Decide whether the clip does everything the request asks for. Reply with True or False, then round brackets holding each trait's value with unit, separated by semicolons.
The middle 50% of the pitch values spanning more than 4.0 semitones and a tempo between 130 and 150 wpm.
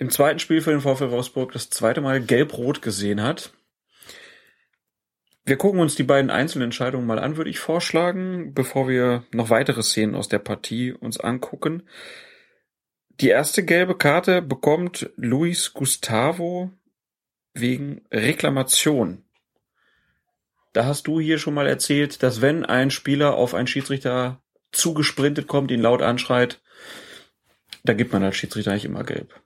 True (4.6 semitones; 145 wpm)